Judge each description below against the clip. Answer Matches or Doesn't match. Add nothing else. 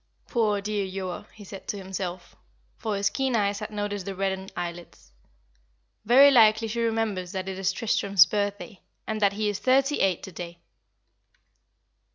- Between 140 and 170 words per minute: Matches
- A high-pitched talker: Matches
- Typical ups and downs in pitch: Doesn't match